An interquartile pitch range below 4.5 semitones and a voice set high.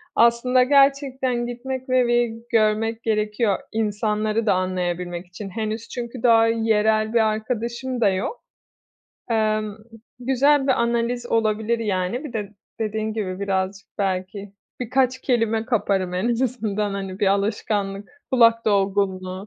Yes: average, 3.0 semitones; high, 220 Hz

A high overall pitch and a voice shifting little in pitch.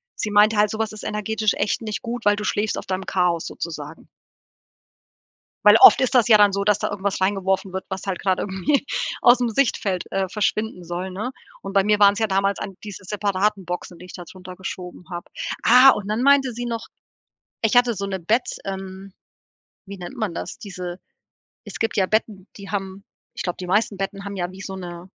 Yes: high, 200 Hz; narrow, 2.3 semitones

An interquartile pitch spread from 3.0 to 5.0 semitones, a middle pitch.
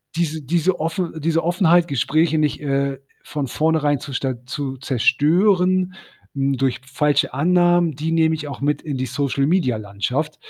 Yes: average, 3.3 semitones; medium, 150 Hz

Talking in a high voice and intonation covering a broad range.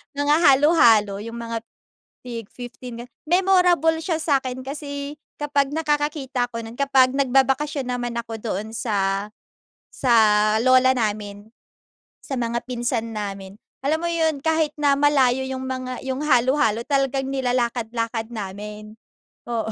No: very high, 255 Hz; average, 3.8 semitones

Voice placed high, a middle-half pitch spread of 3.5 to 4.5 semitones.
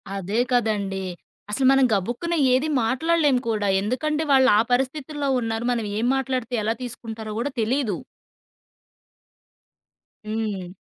Yes: high, 240 Hz; average, 3.8 semitones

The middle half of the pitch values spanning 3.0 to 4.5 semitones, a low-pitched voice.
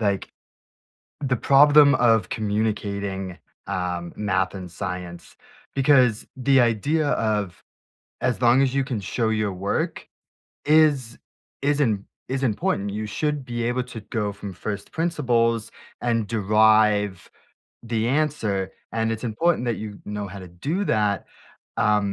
Yes: average, 4.2 semitones; low, 110 Hz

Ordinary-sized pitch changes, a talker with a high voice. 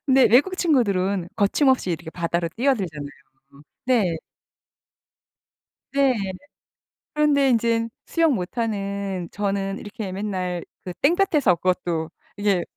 No: wide, 6.2 semitones; high, 200 Hz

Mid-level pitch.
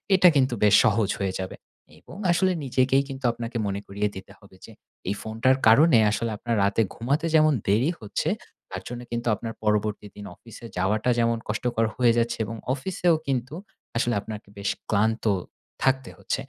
No: low, 115 Hz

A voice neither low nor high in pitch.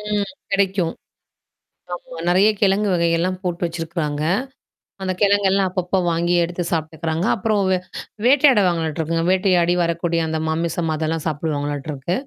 Yes: medium, 175 Hz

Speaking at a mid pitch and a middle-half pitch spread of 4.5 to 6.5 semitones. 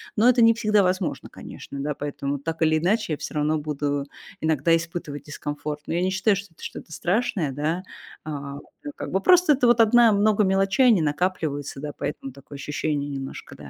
Yes: medium, 160 Hz; wide, 5.4 semitones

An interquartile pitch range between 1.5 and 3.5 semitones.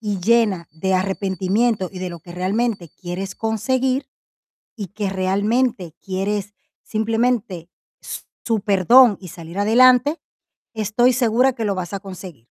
No: average, 3.9 semitones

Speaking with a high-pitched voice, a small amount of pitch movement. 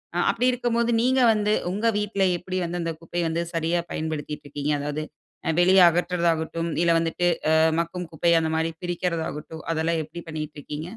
No: medium, 170 Hz; narrow, 2.1 semitones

